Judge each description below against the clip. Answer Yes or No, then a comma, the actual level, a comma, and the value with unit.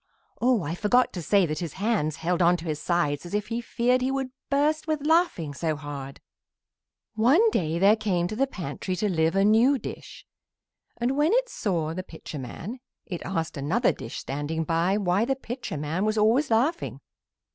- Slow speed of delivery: No, average, 190 wpm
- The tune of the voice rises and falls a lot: Yes, wide, 7.2 semitones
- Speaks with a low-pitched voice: No, high, 195 Hz